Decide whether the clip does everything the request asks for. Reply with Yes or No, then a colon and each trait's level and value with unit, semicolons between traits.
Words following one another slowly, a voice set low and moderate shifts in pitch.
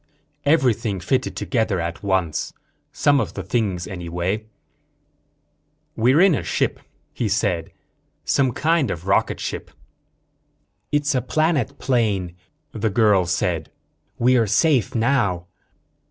No: slow, 115 wpm; low, 110 Hz; wide, 6.2 semitones